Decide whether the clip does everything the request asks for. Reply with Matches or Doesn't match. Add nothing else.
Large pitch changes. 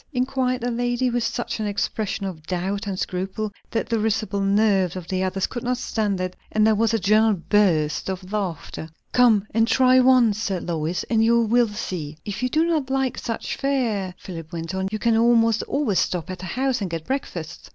Doesn't match